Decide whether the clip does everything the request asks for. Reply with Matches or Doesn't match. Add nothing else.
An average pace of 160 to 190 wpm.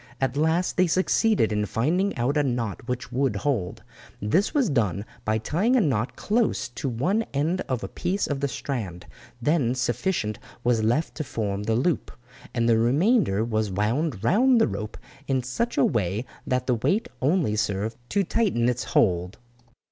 Matches